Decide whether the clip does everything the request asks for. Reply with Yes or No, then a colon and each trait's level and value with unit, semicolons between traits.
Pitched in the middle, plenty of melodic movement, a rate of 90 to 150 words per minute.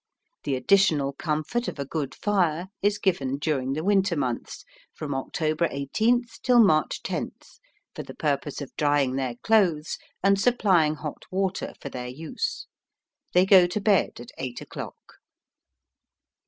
Yes: medium, 155 Hz; wide, 6.0 semitones; average, 145 wpm